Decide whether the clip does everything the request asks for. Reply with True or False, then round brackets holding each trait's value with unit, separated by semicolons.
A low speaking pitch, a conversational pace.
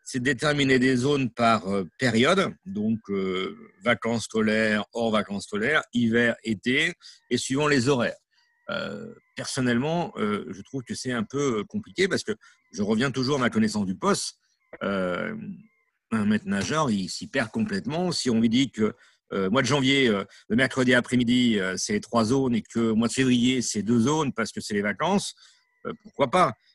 True (130 Hz; 185 wpm)